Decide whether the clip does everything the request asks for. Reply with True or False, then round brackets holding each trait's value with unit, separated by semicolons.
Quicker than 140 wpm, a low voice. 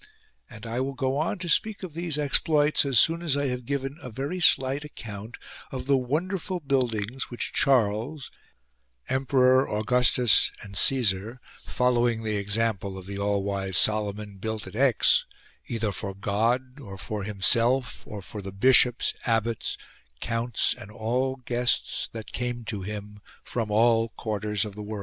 True (160 wpm; 120 Hz)